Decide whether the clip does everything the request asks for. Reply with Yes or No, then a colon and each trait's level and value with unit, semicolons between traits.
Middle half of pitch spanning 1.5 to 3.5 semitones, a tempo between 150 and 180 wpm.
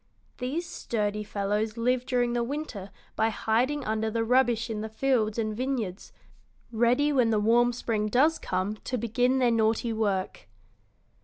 Yes: average, 2.7 semitones; average, 155 wpm